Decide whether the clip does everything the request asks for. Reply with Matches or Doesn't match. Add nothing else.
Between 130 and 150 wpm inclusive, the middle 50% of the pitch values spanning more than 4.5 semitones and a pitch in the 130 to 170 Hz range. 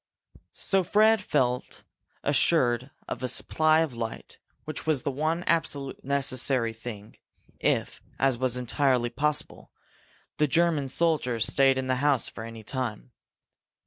Doesn't match